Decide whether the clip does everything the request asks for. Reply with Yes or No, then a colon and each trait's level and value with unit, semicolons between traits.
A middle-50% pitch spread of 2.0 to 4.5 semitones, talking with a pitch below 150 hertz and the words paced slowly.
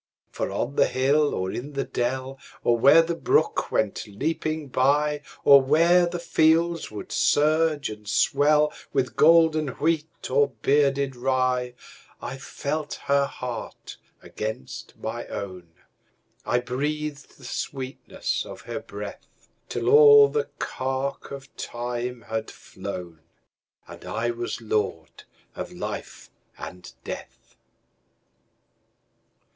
Yes: average, 3.9 semitones; medium, 140 Hz; slow, 105 wpm